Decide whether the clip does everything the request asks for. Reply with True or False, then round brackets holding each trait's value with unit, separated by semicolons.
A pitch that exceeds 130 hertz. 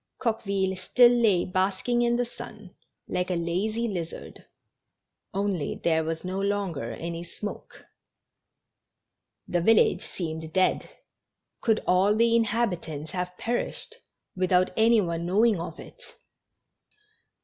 True (190 Hz)